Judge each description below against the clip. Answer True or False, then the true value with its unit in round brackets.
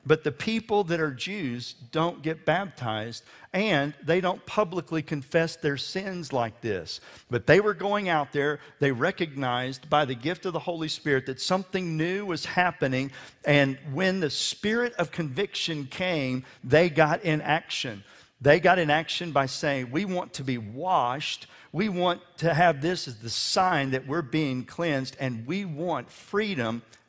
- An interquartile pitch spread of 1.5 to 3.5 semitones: False (4.7 semitones)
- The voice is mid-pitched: True (155 Hz)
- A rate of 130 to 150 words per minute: False (170 wpm)